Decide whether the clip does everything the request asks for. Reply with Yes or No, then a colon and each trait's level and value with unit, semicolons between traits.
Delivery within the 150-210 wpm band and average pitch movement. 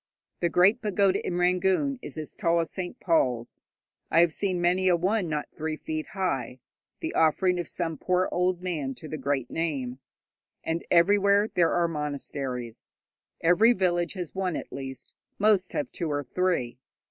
Yes: average, 170 wpm; average, 3.6 semitones